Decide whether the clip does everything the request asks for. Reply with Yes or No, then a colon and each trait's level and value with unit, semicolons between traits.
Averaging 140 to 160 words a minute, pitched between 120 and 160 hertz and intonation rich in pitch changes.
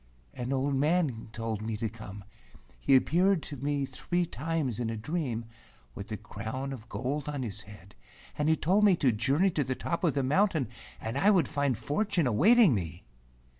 No: average, 190 wpm; low, 135 Hz; wide, 6.1 semitones